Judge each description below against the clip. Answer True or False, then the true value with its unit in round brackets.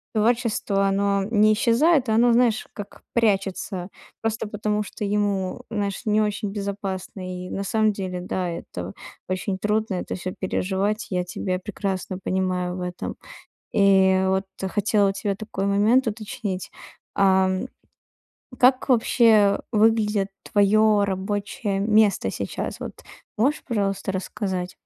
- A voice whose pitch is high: True (200 Hz)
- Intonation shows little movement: True (2.2 semitones)